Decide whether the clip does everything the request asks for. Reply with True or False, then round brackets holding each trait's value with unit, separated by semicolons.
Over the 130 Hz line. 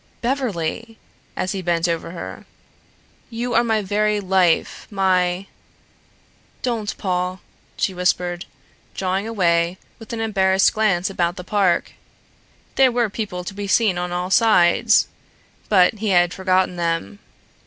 True (190 Hz)